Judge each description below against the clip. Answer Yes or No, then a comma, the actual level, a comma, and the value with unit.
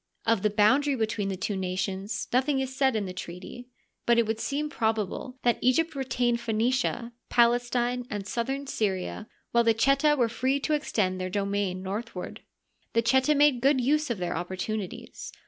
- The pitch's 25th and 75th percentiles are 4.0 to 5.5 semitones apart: Yes, average, 4.5 semitones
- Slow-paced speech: No, average, 170 wpm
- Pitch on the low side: No, high, 235 Hz